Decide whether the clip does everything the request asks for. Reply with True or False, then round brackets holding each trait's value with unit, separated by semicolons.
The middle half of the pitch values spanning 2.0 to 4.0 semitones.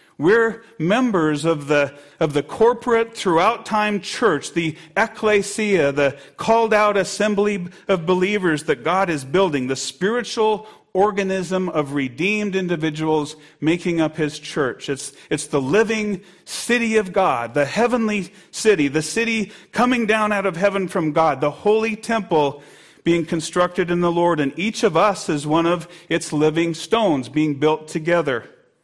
False (5.3 semitones)